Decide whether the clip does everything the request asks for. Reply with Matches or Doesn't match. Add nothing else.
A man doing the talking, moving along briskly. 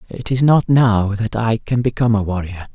Matches